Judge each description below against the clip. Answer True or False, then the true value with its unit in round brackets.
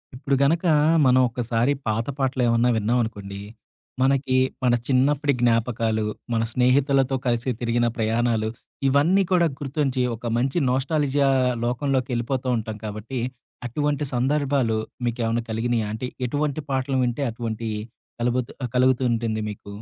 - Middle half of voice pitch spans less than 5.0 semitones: True (3.0 semitones)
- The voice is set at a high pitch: False (125 Hz)